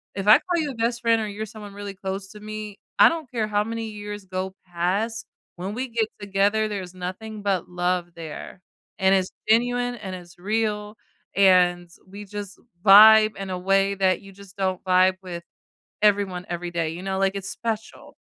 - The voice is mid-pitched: No, high, 200 Hz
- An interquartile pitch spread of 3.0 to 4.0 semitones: No, narrow, 2.5 semitones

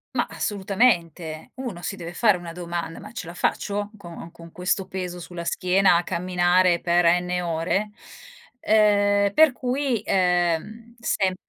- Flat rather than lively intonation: No, average, 3.0 semitones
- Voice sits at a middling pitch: Yes, medium, 180 Hz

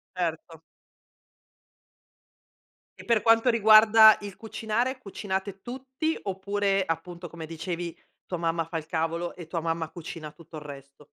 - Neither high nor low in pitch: Yes, medium, 180 Hz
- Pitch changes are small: No, average, 4.7 semitones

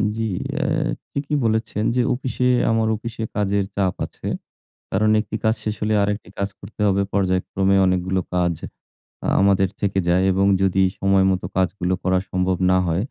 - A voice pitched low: Yes, low, 100 Hz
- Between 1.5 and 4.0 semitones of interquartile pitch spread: Yes, average, 2.7 semitones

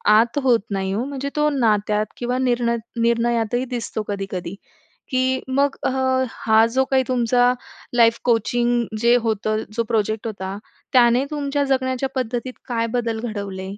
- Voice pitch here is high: Yes, high, 235 Hz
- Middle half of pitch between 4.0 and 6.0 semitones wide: No, average, 2.8 semitones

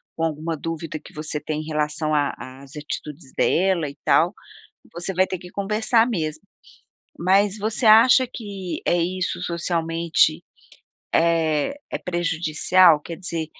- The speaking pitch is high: No, medium, 170 Hz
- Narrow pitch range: No, average, 3.5 semitones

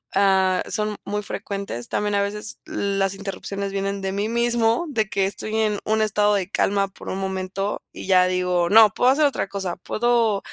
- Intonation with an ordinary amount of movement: No, narrow, 1.9 semitones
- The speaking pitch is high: Yes, high, 200 Hz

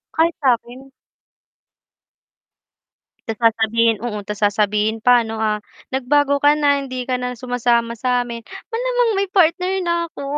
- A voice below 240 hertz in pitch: No, high, 245 Hz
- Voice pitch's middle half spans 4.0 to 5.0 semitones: Yes, average, 4.4 semitones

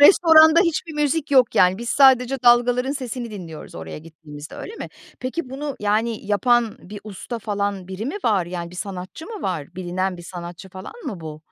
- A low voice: No, high, 210 Hz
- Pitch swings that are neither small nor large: No, wide, 6.6 semitones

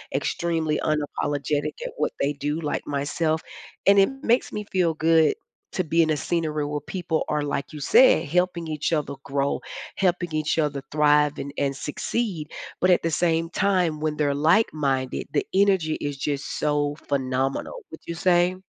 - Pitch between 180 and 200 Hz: No, medium, 155 Hz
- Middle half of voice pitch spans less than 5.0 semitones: Yes, average, 2.8 semitones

